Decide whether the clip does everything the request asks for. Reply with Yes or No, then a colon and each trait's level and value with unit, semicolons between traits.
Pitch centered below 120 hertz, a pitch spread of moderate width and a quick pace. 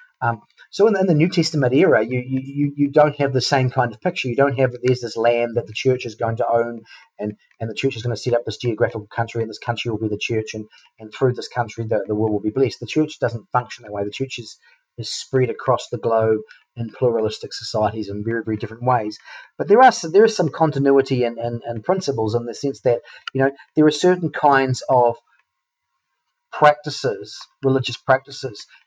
No: low, 125 Hz; average, 3.4 semitones; fast, 230 wpm